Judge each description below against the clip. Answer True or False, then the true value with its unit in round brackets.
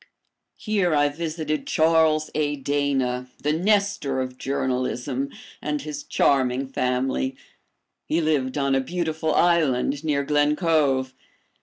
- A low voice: False (145 Hz)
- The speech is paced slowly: True (120 wpm)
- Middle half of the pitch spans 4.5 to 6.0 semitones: False (3.1 semitones)